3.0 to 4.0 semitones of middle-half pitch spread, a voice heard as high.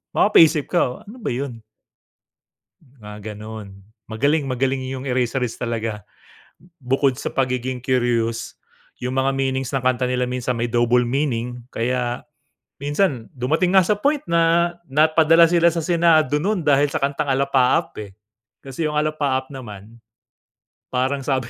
No: average, 3.7 semitones; low, 130 Hz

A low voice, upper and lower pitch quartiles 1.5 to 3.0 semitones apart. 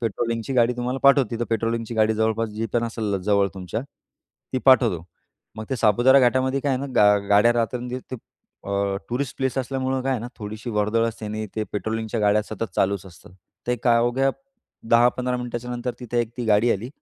Yes: low, 115 Hz; narrow, 2.5 semitones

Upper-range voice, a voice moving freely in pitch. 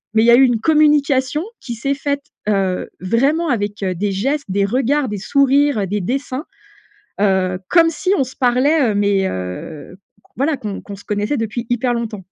Yes: high, 240 Hz; wide, 5.7 semitones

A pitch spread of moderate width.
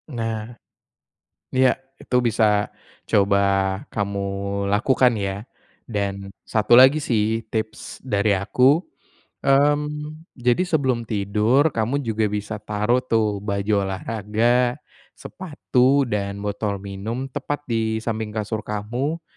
Yes: average, 3.7 semitones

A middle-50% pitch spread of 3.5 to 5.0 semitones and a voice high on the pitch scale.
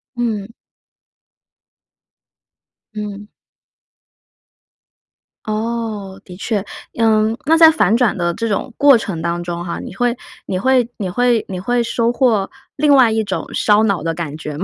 Yes: average, 4.0 semitones; high, 215 Hz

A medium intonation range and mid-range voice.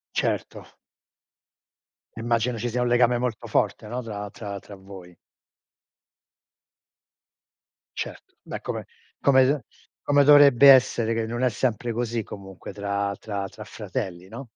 No: average, 3.7 semitones; low, 115 Hz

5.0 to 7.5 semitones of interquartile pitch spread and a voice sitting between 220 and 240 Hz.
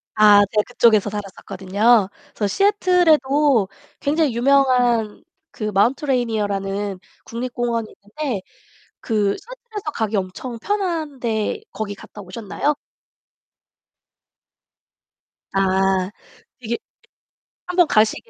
Yes: wide, 5.5 semitones; high, 230 Hz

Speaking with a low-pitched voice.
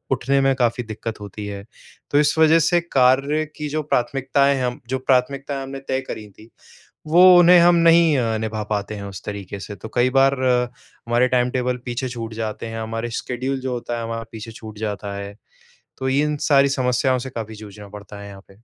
Yes: low, 125 Hz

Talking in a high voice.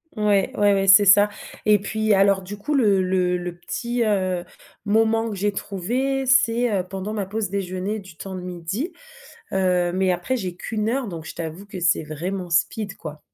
Yes: high, 195 Hz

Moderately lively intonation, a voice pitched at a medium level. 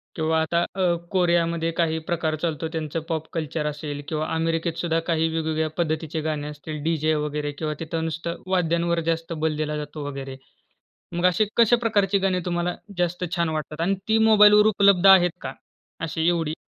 No: narrow, 2.1 semitones; medium, 165 Hz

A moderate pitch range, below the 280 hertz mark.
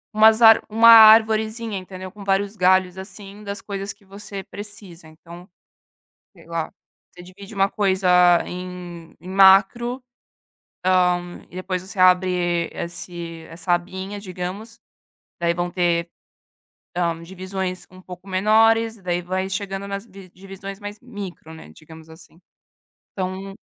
No: narrow, 2.3 semitones; high, 190 Hz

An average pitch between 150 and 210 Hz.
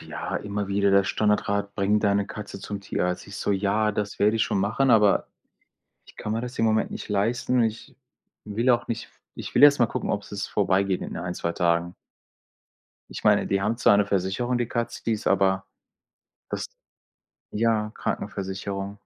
No: low, 105 Hz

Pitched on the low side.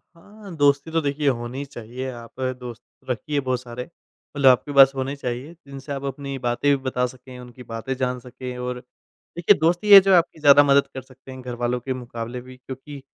Yes: low, 130 Hz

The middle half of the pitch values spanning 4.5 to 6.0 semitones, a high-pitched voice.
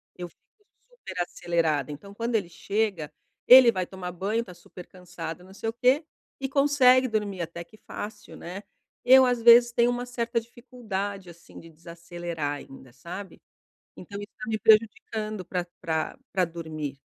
Yes: wide, 5.5 semitones; high, 200 Hz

